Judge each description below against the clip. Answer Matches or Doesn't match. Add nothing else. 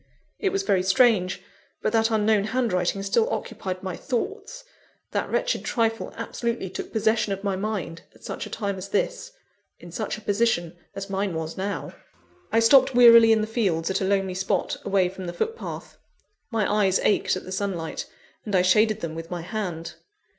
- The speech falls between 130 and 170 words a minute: Doesn't match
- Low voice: Doesn't match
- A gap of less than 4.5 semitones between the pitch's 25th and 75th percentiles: Matches